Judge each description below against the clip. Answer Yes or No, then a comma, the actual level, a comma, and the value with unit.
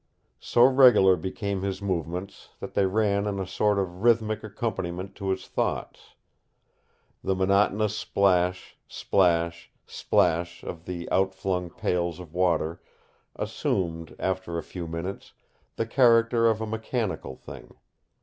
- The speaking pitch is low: Yes, very low, 95 Hz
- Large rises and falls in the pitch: No, average, 3.3 semitones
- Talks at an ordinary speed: No, slow, 130 wpm